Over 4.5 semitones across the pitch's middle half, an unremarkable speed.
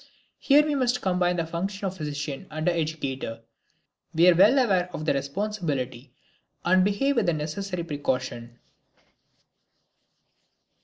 No: wide, 5.4 semitones; slow, 125 wpm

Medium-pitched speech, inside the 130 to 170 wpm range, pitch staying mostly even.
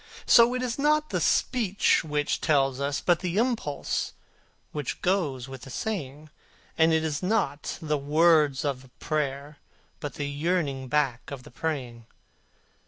No: medium, 150 Hz; average, 150 wpm; average, 4.4 semitones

